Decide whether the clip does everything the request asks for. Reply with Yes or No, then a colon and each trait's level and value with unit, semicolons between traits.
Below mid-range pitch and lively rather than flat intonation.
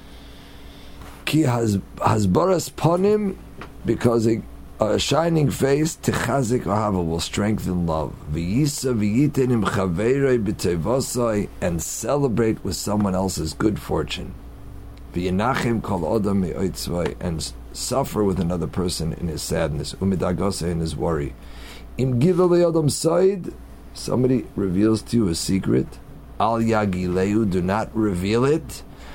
Yes: low, 105 Hz; wide, 6.2 semitones